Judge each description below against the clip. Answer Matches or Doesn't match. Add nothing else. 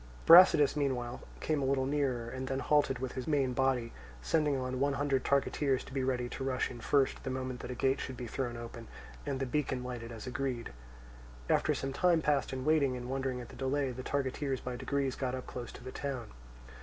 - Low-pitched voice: Matches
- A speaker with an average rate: Doesn't match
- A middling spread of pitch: Doesn't match